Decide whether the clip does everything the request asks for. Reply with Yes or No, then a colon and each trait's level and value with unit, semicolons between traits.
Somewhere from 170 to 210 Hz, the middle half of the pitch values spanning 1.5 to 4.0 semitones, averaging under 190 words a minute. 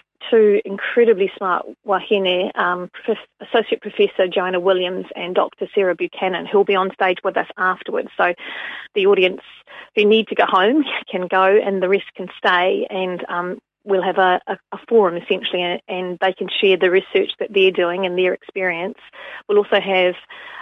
Yes: high, 190 Hz; average, 2.7 semitones; average, 180 wpm